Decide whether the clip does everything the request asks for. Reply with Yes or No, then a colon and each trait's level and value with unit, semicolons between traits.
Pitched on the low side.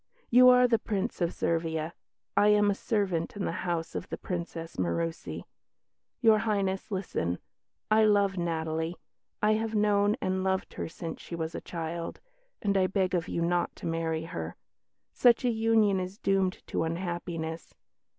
No: medium, 185 Hz